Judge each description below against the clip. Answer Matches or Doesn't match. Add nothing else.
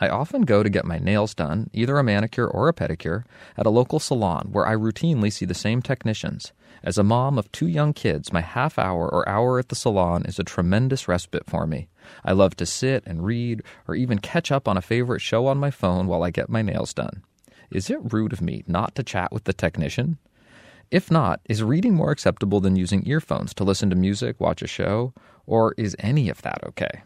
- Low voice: Matches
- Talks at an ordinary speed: Doesn't match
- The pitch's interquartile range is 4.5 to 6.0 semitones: Matches